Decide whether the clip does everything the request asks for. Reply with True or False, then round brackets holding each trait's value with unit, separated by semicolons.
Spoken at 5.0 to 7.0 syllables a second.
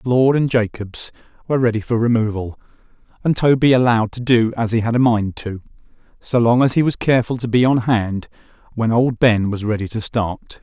True (5.4 syllables/s)